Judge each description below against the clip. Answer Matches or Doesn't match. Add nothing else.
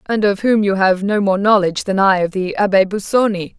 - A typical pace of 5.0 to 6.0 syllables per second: Matches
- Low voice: Doesn't match